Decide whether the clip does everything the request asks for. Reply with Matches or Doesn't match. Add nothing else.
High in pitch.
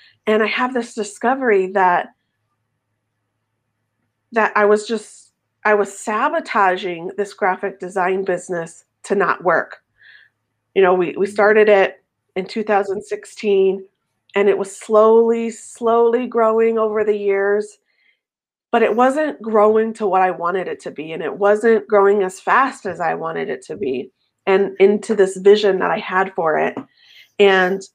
Matches